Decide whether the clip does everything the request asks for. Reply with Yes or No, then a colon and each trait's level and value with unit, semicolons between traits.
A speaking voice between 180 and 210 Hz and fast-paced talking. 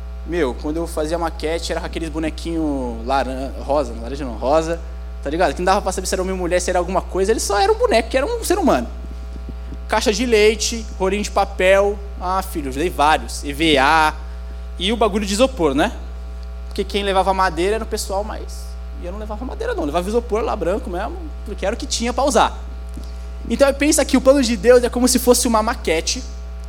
Yes: medium, 185 Hz; fast, 215 wpm